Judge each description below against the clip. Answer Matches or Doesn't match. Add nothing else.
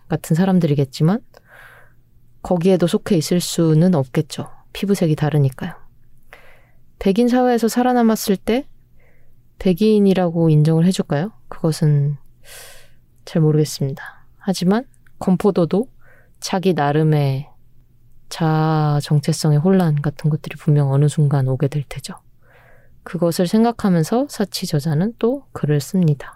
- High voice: Doesn't match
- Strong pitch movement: Doesn't match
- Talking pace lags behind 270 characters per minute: Doesn't match